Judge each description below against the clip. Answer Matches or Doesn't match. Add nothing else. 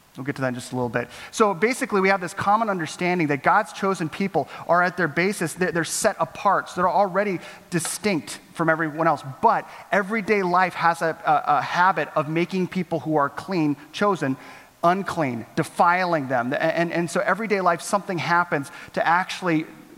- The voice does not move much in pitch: Doesn't match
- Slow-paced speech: Doesn't match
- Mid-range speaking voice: Matches